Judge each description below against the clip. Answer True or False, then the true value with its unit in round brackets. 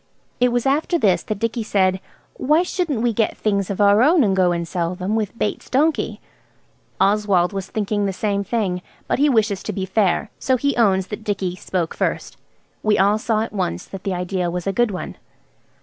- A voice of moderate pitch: False (205 Hz)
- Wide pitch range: False (3.4 semitones)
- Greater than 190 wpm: True (200 wpm)